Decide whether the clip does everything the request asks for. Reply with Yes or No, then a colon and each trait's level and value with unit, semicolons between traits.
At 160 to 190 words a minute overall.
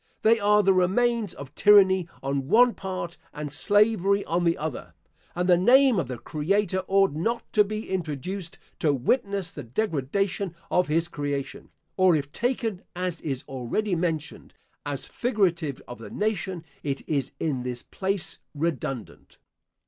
No: average, 150 wpm